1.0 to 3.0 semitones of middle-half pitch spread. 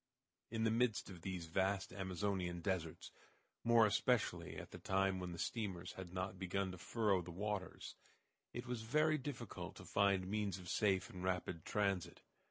Yes: average, 2.7 semitones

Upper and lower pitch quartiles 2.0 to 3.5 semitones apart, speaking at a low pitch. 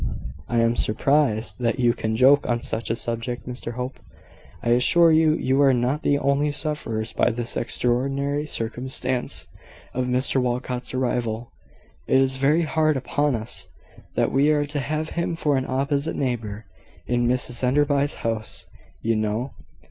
Yes: average, 3.1 semitones; low, 130 Hz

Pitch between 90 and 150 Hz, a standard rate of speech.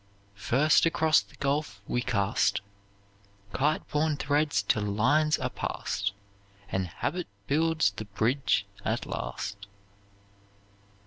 No: low, 135 Hz; slow, 110 wpm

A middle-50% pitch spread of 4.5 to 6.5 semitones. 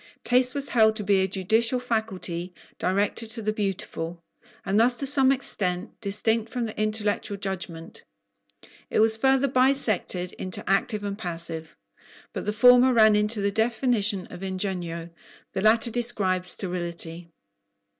No: average, 3.9 semitones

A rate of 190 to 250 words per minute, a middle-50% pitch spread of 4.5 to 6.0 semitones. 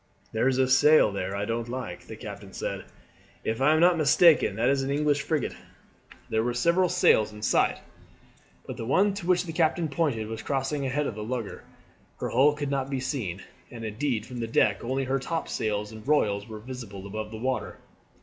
Yes: fast, 205 wpm; average, 5.2 semitones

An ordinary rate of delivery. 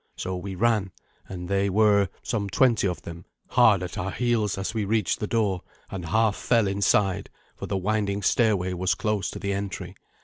Yes: average, 190 wpm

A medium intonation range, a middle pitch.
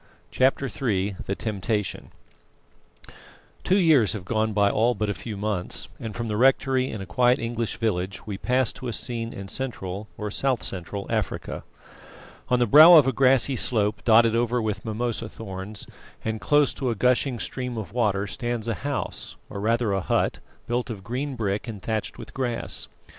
No: average, 3.3 semitones; low, 115 Hz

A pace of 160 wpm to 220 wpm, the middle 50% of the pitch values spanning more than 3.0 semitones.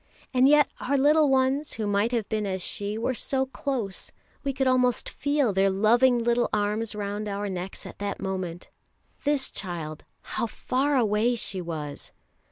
Yes: average, 170 wpm; average, 4.7 semitones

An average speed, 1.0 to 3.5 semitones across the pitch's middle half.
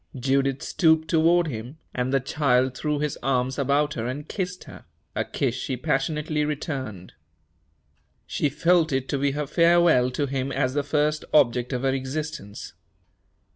Yes: average, 160 wpm; average, 2.9 semitones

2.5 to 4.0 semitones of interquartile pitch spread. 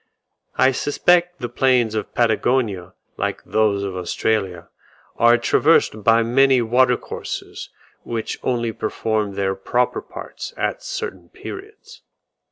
Yes: average, 3.4 semitones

